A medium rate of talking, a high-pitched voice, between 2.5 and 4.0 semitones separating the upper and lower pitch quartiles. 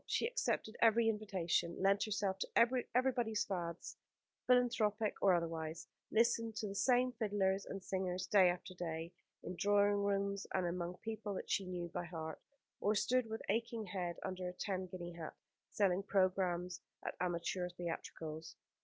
Yes: average, 155 wpm; high, 195 Hz; average, 3.5 semitones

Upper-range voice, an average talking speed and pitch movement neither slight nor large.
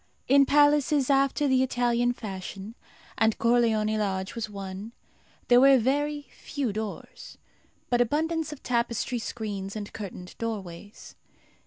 No: high, 235 Hz; slow, 125 wpm; average, 4.6 semitones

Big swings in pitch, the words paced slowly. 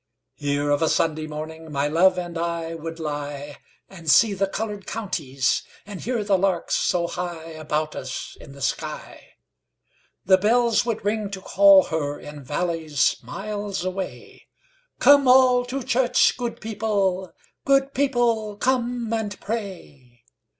Yes: wide, 6.0 semitones; slow, 120 wpm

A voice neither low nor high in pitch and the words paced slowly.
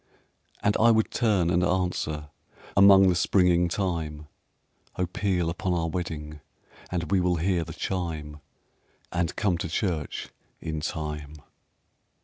No: very low, 85 Hz; slow, 130 wpm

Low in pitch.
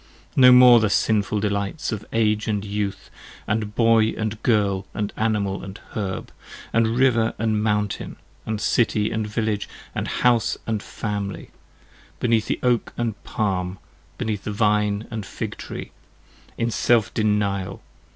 Yes: low, 105 Hz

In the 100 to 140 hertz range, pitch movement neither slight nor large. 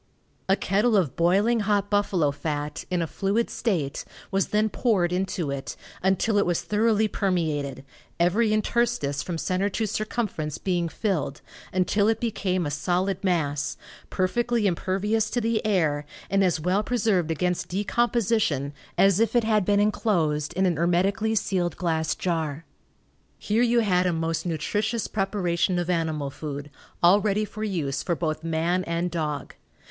No: medium, 185 Hz; average, 4.4 semitones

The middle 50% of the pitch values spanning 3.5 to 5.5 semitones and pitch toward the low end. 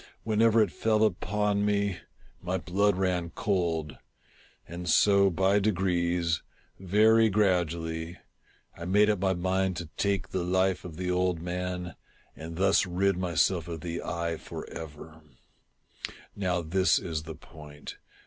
No: narrow, 2.6 semitones; very low, 90 Hz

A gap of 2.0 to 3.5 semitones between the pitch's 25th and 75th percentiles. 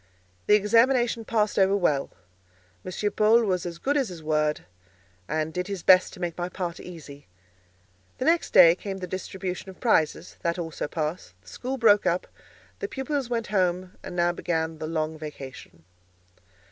No: average, 4.5 semitones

